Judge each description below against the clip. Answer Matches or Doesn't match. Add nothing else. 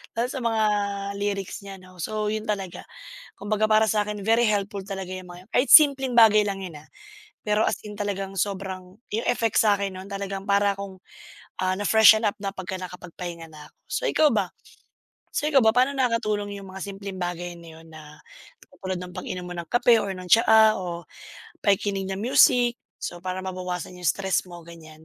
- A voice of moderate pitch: Doesn't match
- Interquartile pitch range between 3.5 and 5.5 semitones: Doesn't match